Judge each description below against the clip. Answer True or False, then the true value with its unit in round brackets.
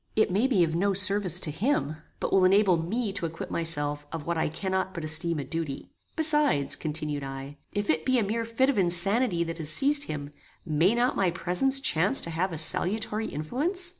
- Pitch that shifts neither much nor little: False (5.7 semitones)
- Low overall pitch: False (180 Hz)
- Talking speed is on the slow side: False (205 wpm)